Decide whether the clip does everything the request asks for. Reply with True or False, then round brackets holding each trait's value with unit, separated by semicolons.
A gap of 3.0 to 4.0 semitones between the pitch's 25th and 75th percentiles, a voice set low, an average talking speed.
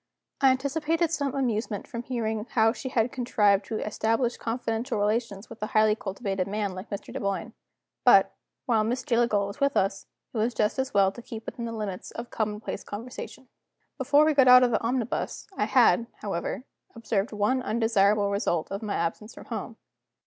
False (3.4 semitones; 225 Hz; 180 wpm)